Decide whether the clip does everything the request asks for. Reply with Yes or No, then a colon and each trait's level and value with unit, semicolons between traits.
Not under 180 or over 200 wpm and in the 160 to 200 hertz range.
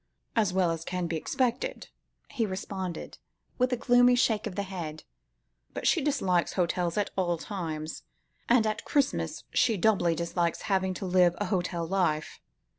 No: average, 160 wpm; medium, 185 Hz